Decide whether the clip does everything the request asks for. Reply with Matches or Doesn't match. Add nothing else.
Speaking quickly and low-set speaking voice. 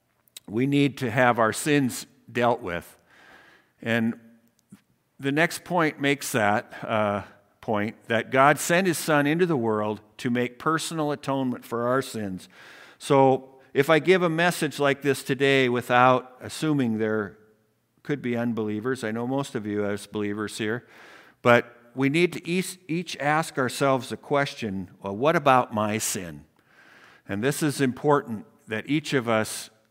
Doesn't match